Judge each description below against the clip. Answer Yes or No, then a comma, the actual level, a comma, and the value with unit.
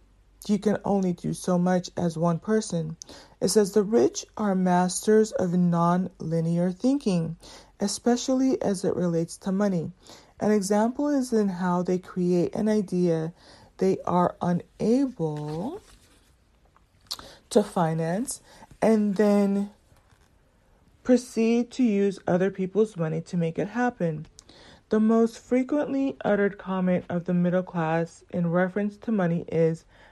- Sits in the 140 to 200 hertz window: Yes, high, 190 Hz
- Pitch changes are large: No, average, 4.0 semitones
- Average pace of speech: No, slow, 130 wpm